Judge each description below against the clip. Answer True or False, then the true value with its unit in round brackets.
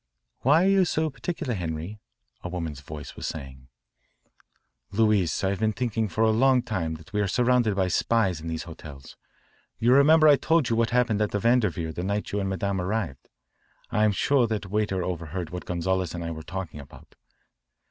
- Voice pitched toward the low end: True (100 Hz)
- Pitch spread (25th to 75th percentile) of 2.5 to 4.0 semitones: False (5.5 semitones)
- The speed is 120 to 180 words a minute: False (190 wpm)